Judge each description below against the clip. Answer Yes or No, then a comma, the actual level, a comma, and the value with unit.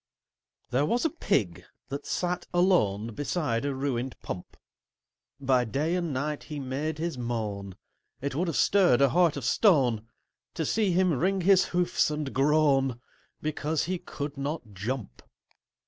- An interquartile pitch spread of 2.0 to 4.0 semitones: No, wide, 5.4 semitones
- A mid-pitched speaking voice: Yes, medium, 145 Hz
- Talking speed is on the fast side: No, average, 150 wpm